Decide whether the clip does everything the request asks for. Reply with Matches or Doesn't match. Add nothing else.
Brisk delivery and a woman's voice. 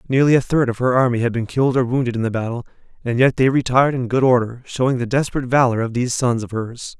Doesn't match